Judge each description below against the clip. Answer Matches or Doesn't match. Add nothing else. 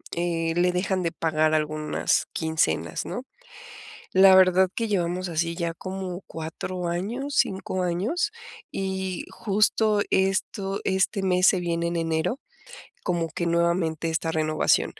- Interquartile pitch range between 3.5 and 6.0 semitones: Doesn't match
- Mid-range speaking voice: Matches